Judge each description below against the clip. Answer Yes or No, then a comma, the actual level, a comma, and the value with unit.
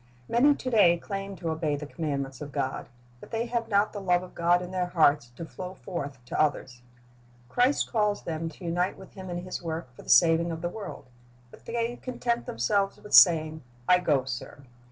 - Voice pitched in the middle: Yes, medium, 175 Hz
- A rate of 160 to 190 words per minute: No, fast, 205 wpm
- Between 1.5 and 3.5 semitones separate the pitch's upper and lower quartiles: No, average, 4.4 semitones